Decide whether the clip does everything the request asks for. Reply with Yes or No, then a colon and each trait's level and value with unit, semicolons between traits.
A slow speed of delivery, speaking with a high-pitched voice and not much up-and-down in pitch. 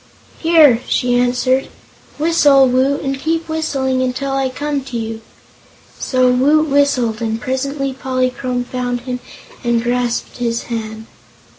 Yes: slow, 130 wpm; very high, 255 Hz; narrow, 2.2 semitones